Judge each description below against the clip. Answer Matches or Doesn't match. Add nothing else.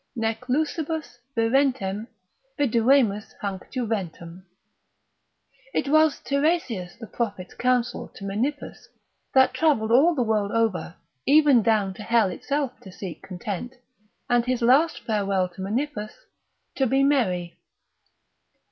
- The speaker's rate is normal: Doesn't match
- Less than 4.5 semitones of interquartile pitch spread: Doesn't match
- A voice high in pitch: Matches